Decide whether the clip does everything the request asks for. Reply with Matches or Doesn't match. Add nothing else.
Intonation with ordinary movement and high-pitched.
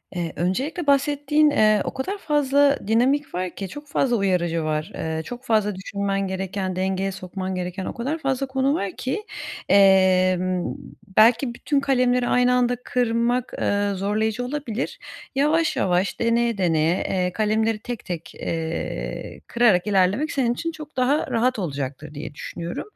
Doesn't match